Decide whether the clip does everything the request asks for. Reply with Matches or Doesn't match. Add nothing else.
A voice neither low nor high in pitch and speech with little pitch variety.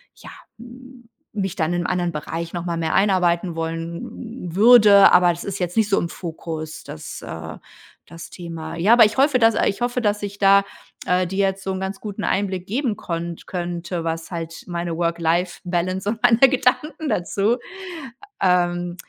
Doesn't match